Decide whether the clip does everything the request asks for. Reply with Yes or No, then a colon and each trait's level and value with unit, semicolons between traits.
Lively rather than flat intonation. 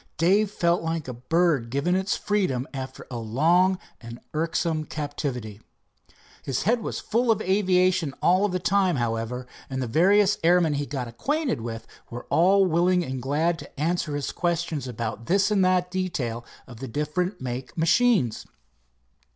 Yes: wide, 6.2 semitones